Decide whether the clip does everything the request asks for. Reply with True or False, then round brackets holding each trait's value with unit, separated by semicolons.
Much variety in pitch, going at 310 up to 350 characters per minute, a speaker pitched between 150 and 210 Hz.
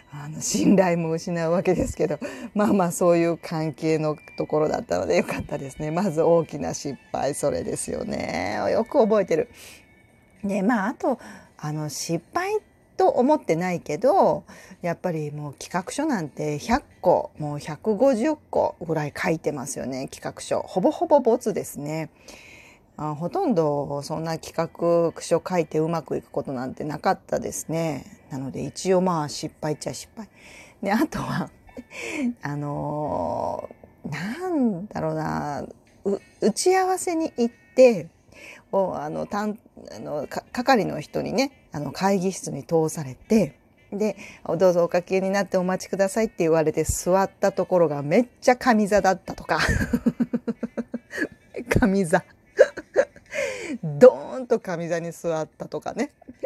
False (7.1 semitones; 275 characters per minute; 185 Hz)